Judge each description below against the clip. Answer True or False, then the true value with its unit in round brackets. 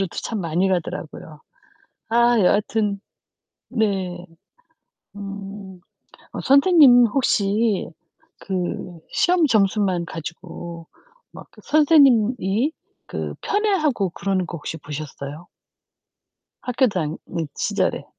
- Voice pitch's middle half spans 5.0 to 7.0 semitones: True (5.4 semitones)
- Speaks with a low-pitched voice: False (200 Hz)